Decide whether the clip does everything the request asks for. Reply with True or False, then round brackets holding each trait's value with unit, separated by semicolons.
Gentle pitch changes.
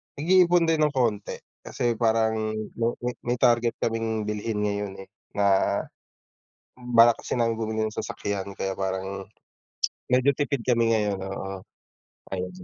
False (3.1 semitones)